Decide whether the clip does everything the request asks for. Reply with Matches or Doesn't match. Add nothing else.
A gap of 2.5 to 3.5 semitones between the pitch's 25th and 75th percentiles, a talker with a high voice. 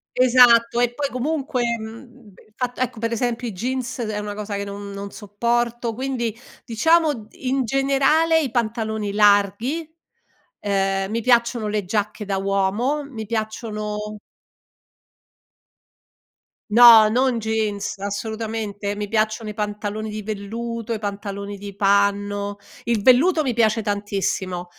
Matches